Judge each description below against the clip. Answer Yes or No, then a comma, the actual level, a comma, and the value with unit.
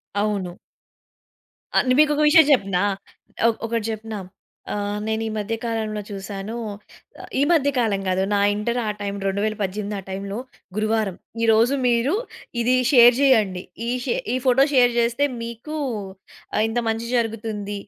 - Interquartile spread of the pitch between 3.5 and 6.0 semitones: No, average, 2.7 semitones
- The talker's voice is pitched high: Yes, high, 220 Hz